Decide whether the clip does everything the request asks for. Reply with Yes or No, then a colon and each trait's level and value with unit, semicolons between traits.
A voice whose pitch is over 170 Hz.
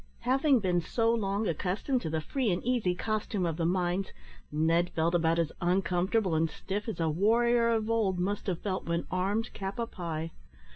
Yes: high, 190 Hz